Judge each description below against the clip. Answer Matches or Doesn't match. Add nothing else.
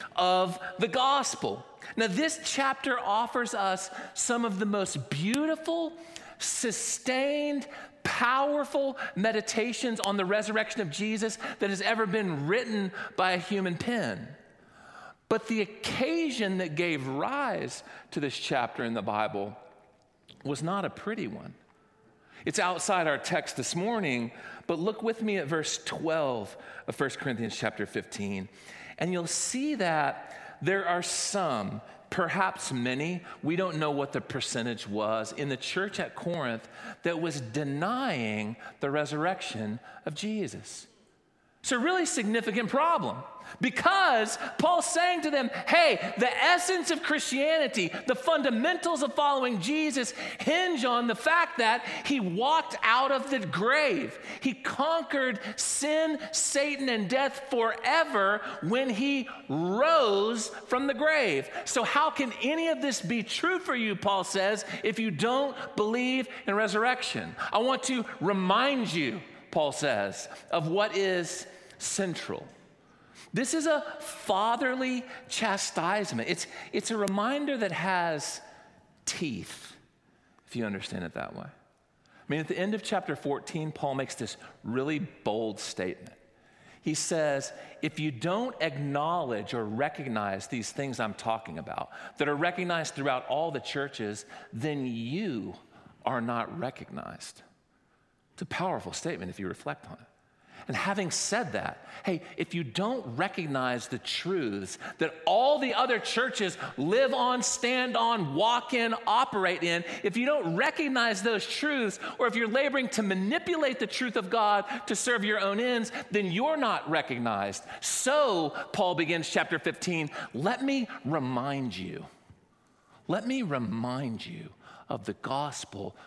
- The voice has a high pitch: Matches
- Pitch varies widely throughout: Matches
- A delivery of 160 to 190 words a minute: Doesn't match